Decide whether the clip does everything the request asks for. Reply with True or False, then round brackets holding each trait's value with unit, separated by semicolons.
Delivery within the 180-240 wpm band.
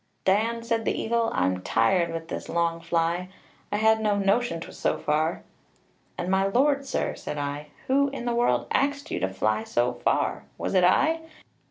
True (185 wpm)